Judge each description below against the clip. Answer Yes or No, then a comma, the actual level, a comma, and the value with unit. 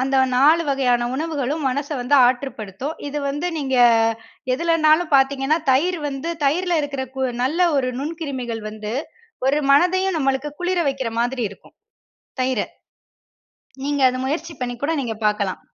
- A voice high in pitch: Yes, very high, 275 Hz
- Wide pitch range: No, average, 3.6 semitones